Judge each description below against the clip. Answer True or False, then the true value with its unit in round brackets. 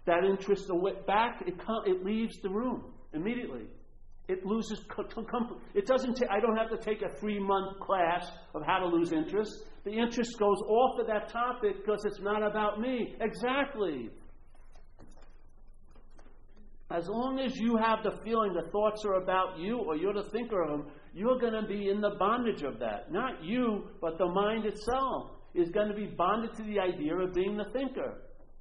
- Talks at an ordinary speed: True (185 wpm)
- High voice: True (210 Hz)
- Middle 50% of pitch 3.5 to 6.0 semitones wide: False (2.9 semitones)